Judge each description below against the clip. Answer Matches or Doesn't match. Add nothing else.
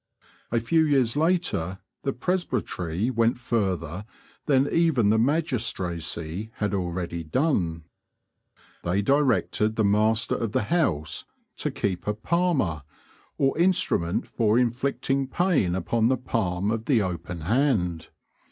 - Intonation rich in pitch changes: Matches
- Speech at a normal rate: Doesn't match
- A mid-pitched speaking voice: Doesn't match